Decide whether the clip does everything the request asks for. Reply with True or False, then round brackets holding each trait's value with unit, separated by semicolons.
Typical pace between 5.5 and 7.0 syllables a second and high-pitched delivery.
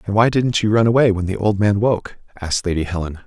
False (6.2 syllables/s; 100 Hz)